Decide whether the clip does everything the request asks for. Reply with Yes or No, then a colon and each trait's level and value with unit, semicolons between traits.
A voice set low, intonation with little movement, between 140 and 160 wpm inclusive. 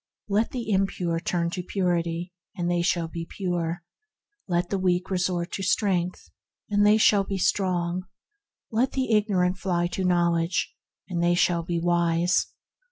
No: medium, 180 Hz; narrow, 2.1 semitones; average, 150 wpm